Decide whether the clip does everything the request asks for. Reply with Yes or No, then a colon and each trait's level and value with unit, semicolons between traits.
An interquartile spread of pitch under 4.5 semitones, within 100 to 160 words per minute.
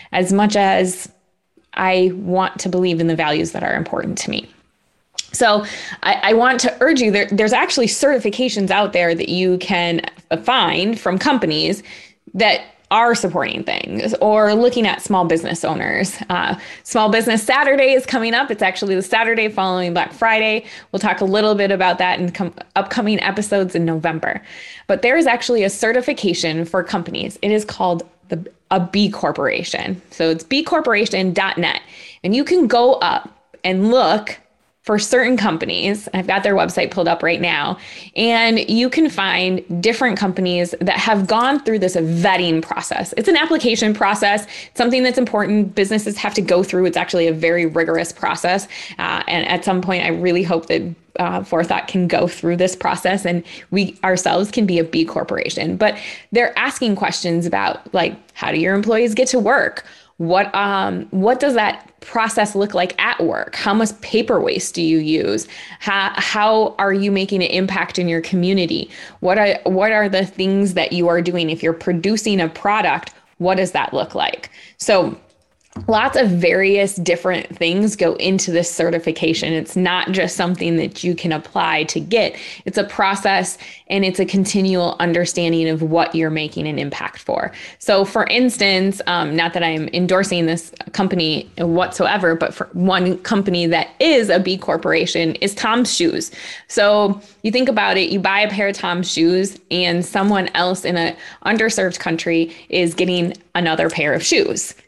No: average, 3.5 semitones; average, 175 wpm